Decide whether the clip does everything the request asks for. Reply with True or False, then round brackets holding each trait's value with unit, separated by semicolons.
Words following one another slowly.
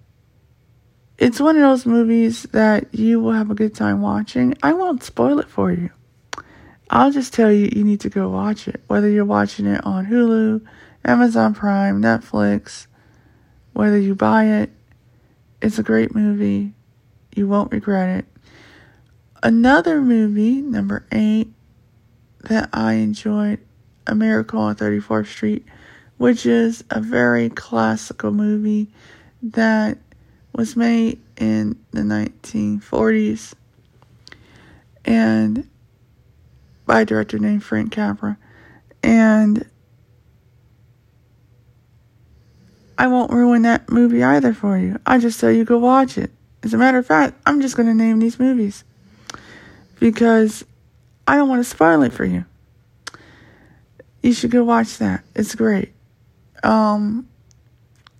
True (130 wpm)